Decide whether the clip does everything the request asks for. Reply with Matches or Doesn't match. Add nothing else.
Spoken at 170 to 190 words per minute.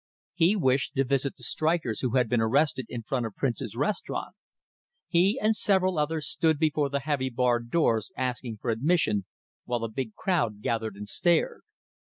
Matches